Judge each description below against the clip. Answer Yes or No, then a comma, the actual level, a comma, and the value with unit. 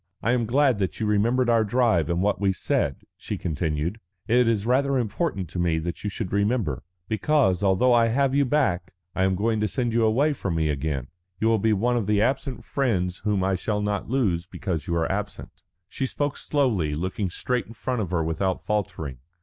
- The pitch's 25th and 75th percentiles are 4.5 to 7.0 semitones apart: Yes, average, 5.1 semitones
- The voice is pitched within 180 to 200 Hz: No, low, 105 Hz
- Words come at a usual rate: No, fast, 215 wpm